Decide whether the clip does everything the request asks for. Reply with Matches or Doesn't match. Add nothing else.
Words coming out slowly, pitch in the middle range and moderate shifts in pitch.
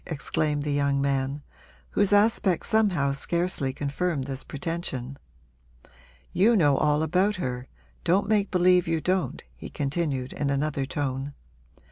Matches